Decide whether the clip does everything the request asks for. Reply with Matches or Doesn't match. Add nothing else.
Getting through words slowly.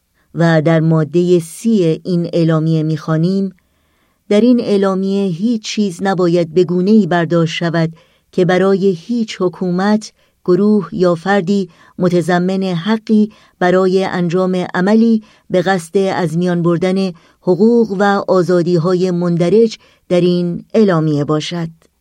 Doesn't match